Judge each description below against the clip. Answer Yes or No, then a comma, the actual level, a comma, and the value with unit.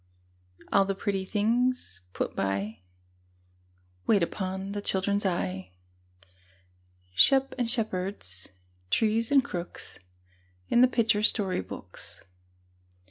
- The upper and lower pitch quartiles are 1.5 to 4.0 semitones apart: No, average, 4.7 semitones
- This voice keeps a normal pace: No, slow, 100 wpm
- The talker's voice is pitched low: No, high, 200 Hz